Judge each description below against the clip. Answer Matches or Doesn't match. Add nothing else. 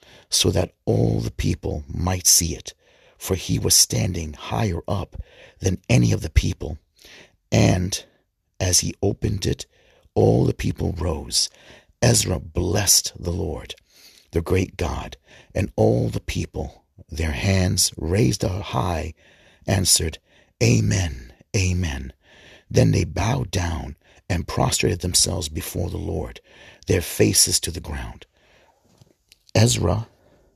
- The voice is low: Matches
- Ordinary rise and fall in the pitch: Matches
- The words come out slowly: Matches